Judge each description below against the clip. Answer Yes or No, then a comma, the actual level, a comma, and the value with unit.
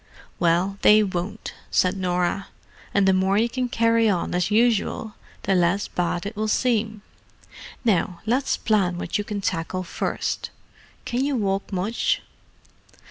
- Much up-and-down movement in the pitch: No, average, 3.4 semitones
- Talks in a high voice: Yes, high, 200 Hz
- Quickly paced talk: No, average, 145 wpm